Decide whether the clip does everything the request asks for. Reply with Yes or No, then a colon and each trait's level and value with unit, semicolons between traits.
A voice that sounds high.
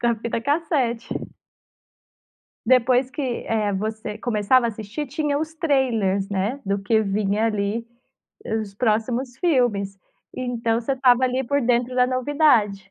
Yes: high, 235 Hz